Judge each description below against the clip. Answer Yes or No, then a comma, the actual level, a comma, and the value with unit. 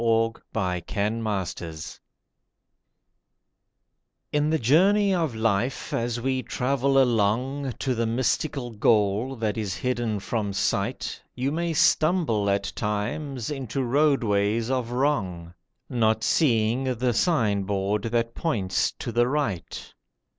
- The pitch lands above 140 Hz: No, low, 115 Hz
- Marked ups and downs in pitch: No, average, 4.4 semitones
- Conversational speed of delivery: No, slow, 120 wpm